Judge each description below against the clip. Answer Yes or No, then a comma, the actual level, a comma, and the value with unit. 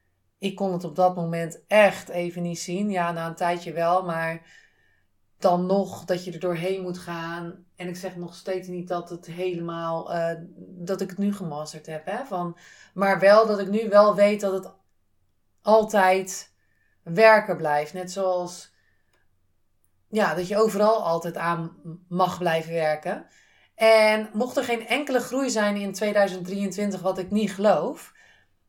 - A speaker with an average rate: Yes, average, 165 wpm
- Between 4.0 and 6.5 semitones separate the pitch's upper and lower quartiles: No, average, 3.2 semitones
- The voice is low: No, medium, 180 Hz